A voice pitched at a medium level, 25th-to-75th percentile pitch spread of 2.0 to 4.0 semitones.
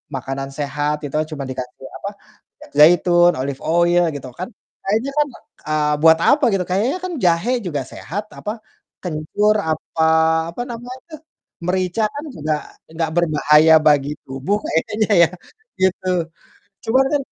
No: medium, 170 Hz; wide, 5.5 semitones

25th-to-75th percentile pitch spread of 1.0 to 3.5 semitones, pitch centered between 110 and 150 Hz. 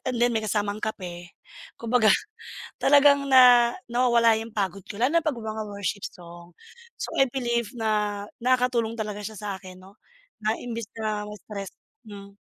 No: average, 2.9 semitones; high, 220 Hz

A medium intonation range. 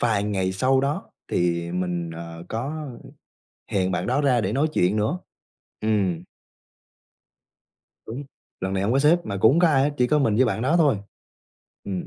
No: wide, 6.6 semitones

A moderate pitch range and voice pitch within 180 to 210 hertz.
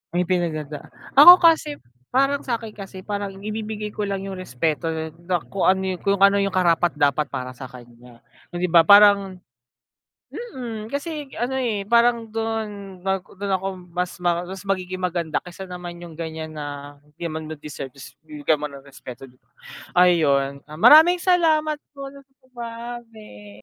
No: wide, 6.1 semitones; medium, 185 Hz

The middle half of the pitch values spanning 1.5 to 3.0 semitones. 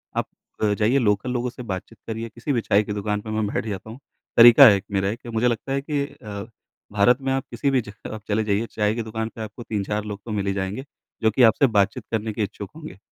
Yes: narrow, 2.5 semitones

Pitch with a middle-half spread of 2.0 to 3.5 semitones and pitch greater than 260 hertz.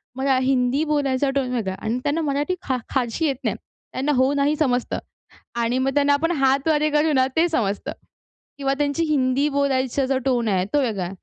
Yes: narrow, 2.4 semitones; very high, 270 Hz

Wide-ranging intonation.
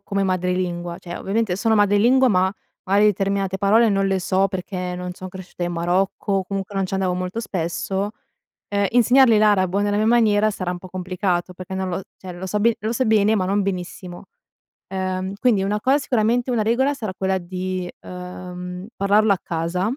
No: narrow, 2.5 semitones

